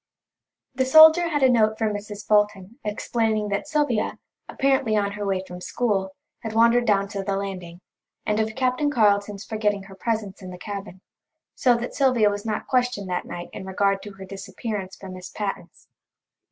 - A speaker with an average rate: Yes, average, 180 wpm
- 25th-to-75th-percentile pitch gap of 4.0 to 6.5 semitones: No, average, 3.1 semitones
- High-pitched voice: Yes, high, 210 Hz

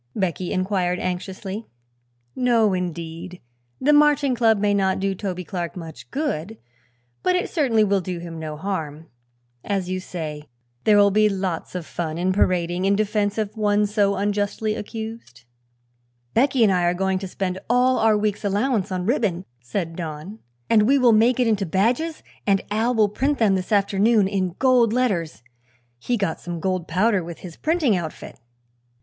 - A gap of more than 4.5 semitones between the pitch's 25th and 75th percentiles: No, average, 3.6 semitones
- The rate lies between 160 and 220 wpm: Yes, average, 170 wpm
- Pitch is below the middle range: No, high, 200 Hz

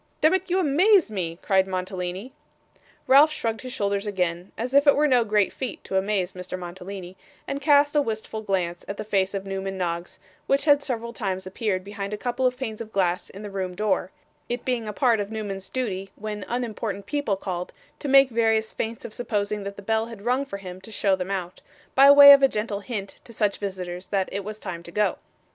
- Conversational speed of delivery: No, fast, 215 wpm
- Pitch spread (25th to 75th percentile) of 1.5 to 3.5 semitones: No, average, 4.3 semitones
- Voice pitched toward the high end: Yes, high, 210 Hz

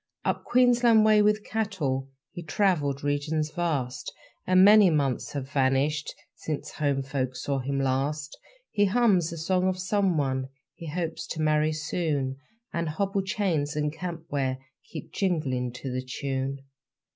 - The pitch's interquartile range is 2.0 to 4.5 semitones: No, average, 5.2 semitones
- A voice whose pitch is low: No, medium, 155 Hz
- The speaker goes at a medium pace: Yes, average, 145 wpm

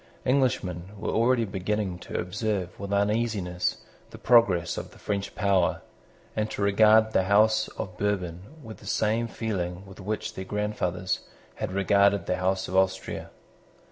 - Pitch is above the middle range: No, low, 100 Hz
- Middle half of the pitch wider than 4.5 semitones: No, average, 2.7 semitones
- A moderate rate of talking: Yes, average, 150 wpm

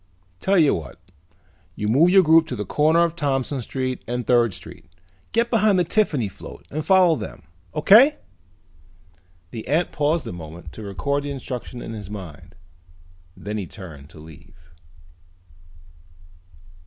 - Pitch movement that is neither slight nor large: No, wide, 8.6 semitones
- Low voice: Yes, low, 130 Hz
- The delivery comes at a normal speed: Yes, average, 150 wpm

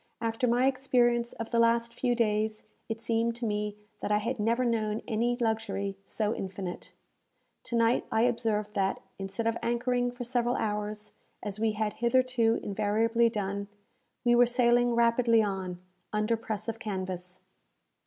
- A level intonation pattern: Yes, narrow, 2.3 semitones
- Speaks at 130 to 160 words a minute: Yes, average, 155 wpm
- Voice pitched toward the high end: Yes, high, 225 Hz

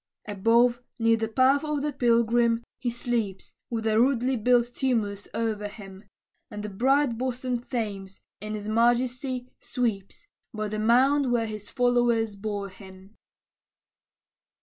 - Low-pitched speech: No, high, 230 Hz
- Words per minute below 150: Yes, slow, 135 wpm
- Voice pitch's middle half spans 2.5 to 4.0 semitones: Yes, average, 2.8 semitones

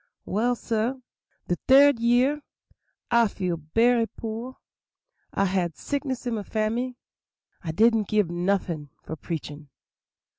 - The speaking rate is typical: No, slow, 115 wpm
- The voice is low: No, high, 220 Hz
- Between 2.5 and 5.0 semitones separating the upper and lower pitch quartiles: No, wide, 5.5 semitones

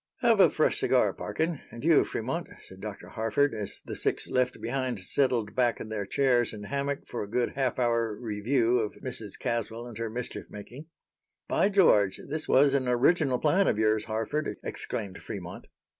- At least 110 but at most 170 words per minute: No, average, 180 wpm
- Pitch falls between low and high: No, low, 120 Hz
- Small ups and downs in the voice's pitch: No, average, 4.2 semitones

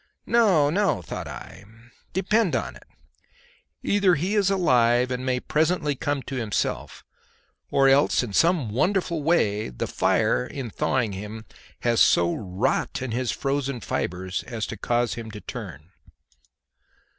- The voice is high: No, low, 130 Hz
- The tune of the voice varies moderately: No, wide, 6.8 semitones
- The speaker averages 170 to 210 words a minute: No, average, 145 wpm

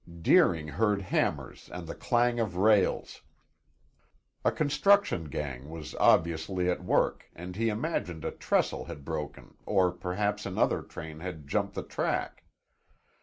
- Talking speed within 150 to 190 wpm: No, slow, 135 wpm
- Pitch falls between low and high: No, very low, 90 Hz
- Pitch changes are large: No, average, 4.6 semitones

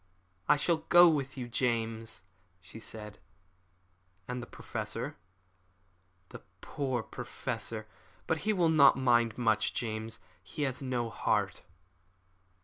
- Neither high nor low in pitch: No, low, 120 Hz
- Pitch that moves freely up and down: No, average, 4.0 semitones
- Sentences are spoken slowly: Yes, slow, 125 wpm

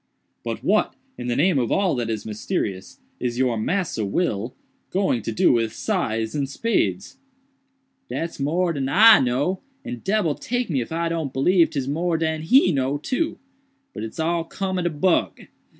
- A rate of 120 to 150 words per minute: No, average, 180 wpm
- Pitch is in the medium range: Yes, medium, 150 Hz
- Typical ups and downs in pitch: No, wide, 6.8 semitones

